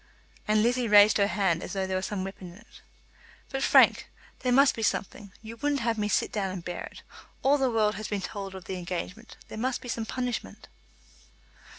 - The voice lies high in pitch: Yes, high, 210 Hz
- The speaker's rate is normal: No, fast, 215 wpm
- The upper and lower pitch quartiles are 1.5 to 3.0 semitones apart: No, average, 3.6 semitones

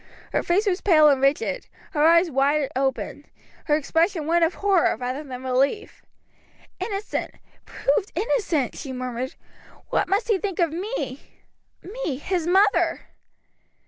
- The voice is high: Yes, very high, 330 Hz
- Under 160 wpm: Yes, average, 140 wpm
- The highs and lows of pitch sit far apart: Yes, wide, 6.2 semitones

